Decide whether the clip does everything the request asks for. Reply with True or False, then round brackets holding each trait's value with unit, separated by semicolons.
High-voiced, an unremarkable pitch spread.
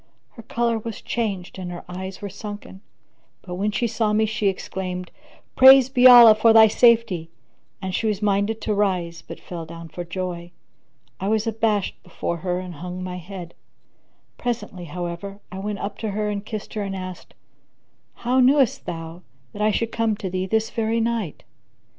True (200 Hz; 3.6 semitones)